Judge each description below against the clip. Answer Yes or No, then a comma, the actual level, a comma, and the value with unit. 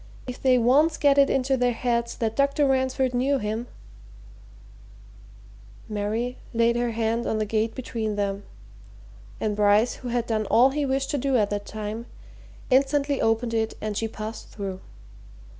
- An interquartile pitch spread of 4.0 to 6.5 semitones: No, average, 3.6 semitones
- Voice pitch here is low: No, high, 230 Hz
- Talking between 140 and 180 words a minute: Yes, average, 165 wpm